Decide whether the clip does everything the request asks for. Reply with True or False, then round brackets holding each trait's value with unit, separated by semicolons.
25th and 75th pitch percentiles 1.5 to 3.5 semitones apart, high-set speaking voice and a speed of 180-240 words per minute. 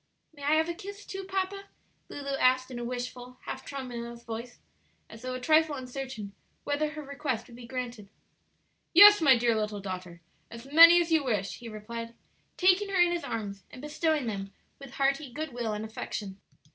False (5.1 semitones; 255 Hz; 185 wpm)